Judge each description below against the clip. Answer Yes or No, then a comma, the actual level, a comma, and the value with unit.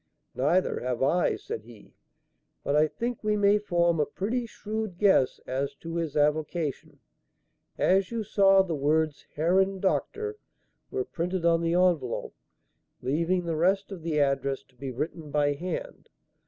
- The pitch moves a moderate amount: Yes, average, 4.9 semitones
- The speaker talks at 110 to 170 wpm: Yes, average, 155 wpm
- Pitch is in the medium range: Yes, medium, 170 Hz